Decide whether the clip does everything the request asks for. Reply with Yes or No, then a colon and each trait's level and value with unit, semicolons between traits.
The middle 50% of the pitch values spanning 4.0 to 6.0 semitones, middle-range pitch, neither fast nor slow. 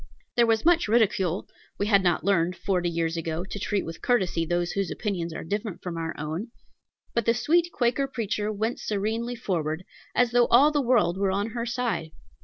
No: average, 5.3 semitones; high, 205 Hz; average, 195 wpm